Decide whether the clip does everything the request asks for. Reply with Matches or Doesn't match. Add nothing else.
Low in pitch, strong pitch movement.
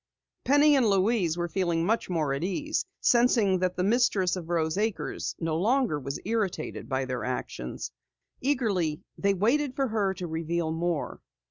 Doesn't match